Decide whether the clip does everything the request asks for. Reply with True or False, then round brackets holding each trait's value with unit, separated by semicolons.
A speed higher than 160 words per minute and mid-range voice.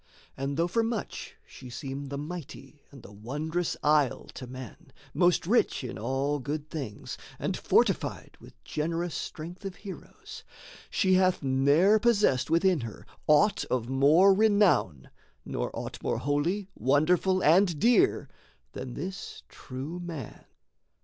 False (135 wpm; 155 Hz)